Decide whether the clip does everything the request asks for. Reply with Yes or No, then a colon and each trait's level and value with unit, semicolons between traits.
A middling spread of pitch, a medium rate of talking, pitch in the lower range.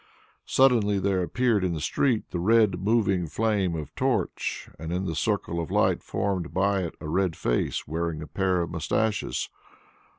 Yes: average, 3.6 semitones; average, 170 wpm; very low, 95 Hz